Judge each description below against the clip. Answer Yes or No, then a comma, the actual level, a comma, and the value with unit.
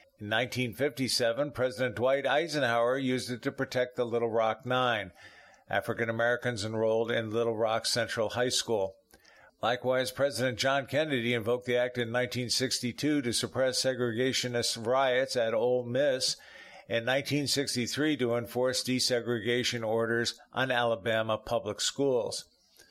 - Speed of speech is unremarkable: No, slow, 125 wpm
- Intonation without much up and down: Yes, narrow, 1.8 semitones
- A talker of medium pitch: No, low, 125 Hz